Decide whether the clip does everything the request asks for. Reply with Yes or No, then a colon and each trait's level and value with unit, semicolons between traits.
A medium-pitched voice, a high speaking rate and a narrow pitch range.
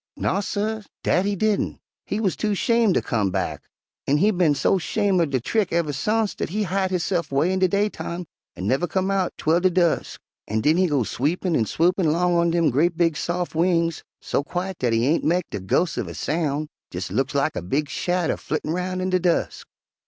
No: medium, 175 Hz; fast, 220 wpm; average, 4.0 semitones